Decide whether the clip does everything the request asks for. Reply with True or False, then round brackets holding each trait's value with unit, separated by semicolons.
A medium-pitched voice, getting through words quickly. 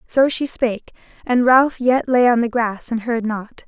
False (240 Hz; 210 wpm)